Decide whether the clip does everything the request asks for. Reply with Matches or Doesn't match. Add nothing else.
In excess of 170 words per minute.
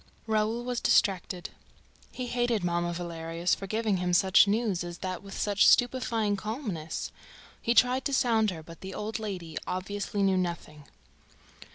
Doesn't match